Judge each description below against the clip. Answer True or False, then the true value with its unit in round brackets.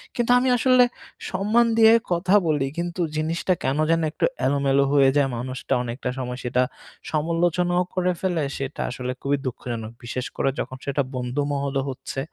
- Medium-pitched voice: True (145 Hz)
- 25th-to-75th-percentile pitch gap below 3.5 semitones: False (4.9 semitones)